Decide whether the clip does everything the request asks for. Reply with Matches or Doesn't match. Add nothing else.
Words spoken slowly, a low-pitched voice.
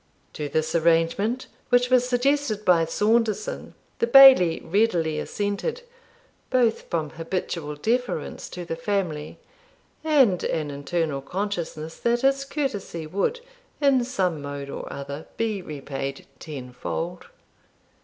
Doesn't match